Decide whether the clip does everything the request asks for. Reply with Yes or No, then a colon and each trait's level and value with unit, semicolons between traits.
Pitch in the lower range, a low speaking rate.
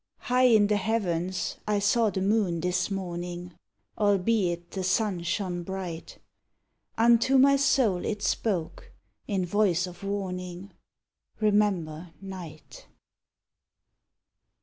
No: high, 190 Hz; slow, 105 wpm